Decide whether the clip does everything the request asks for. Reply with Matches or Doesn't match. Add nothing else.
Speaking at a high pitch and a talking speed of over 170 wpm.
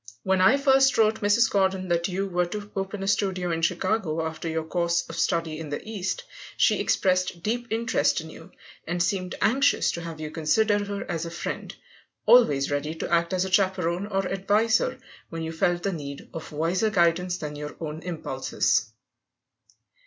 Doesn't match